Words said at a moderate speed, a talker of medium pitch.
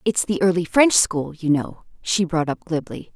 No: fast, 210 wpm; medium, 180 Hz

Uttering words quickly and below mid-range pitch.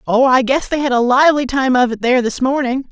No: fast, 270 wpm; very high, 260 Hz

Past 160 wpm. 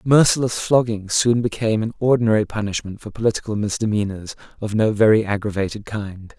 No: average, 140 wpm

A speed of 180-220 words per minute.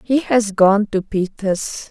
No: average, 160 wpm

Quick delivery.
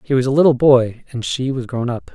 Yes: fast, 280 wpm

